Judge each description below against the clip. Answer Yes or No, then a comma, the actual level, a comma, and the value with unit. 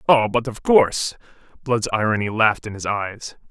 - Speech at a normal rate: Yes, average, 170 wpm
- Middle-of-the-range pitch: No, low, 115 Hz